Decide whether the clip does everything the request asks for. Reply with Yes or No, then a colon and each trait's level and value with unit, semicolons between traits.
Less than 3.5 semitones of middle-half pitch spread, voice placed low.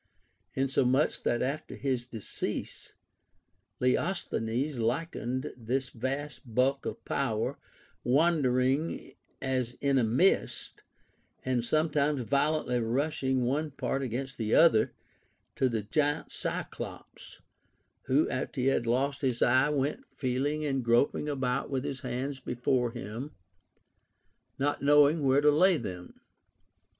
Yes: average, 2.9 semitones; low, 130 Hz